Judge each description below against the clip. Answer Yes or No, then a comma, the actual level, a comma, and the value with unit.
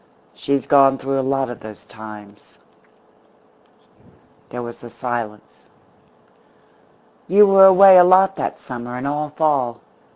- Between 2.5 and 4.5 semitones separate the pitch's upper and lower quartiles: No, average, 4.9 semitones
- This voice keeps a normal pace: No, slow, 130 wpm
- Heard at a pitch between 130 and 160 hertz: Yes, low, 135 Hz